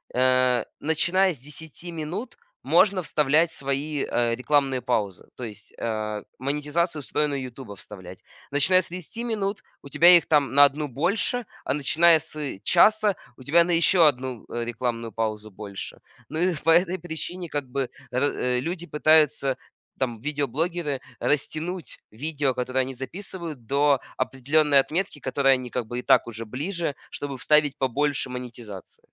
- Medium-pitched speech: Yes, medium, 145 Hz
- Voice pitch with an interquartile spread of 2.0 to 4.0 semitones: No, average, 4.6 semitones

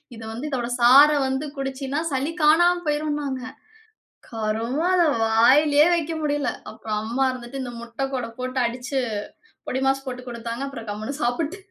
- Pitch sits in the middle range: No, very high, 265 Hz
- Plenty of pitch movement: No, average, 3.6 semitones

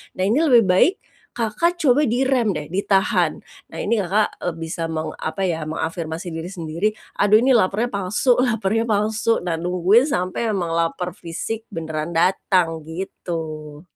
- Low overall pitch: No, medium, 185 Hz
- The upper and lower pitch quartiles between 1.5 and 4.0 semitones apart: No, average, 5.3 semitones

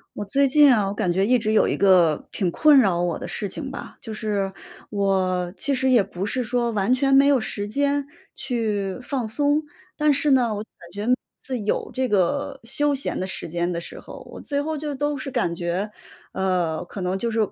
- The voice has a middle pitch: No, high, 220 Hz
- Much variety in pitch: Yes, wide, 6.0 semitones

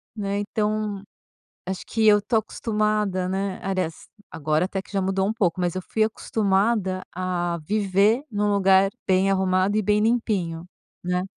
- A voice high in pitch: Yes, high, 195 Hz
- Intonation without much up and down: Yes, narrow, 2.3 semitones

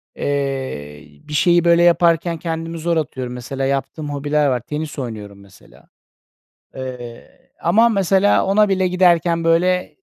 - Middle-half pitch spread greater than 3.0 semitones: Yes, average, 4.6 semitones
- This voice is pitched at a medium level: Yes, medium, 160 Hz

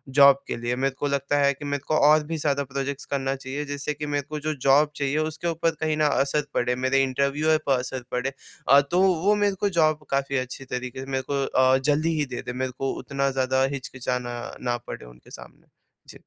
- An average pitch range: No, narrow, 2.2 semitones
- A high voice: No, medium, 140 Hz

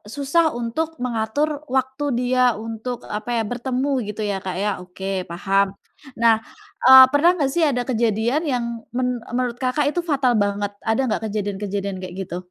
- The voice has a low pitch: No, high, 240 Hz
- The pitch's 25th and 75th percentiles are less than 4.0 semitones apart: No, average, 4.3 semitones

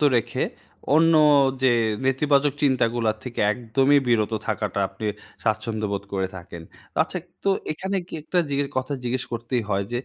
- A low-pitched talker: Yes, low, 120 Hz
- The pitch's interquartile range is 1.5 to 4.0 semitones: No, average, 4.5 semitones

